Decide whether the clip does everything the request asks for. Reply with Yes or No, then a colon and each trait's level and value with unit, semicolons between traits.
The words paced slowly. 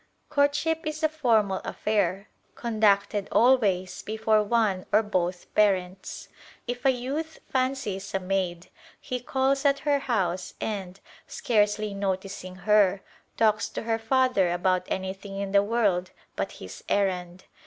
Yes: slow, 130 wpm